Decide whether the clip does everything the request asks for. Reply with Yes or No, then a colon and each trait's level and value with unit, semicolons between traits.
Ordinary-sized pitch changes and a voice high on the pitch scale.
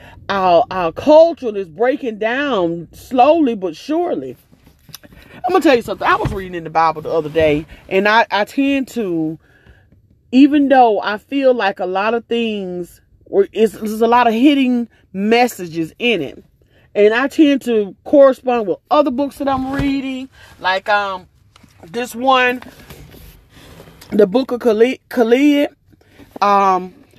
No: wide, 5.9 semitones; high, 230 Hz